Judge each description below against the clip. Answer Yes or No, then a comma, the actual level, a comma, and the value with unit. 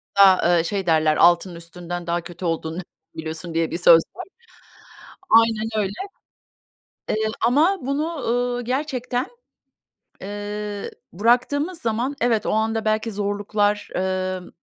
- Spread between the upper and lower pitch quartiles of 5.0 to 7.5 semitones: Yes, wide, 5.5 semitones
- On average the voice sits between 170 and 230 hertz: Yes, high, 205 Hz